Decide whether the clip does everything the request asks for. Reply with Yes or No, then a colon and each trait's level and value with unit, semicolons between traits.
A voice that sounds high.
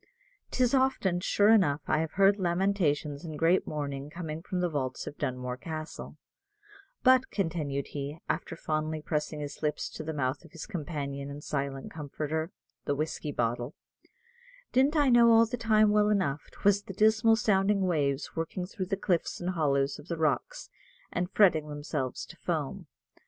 No: medium, 160 Hz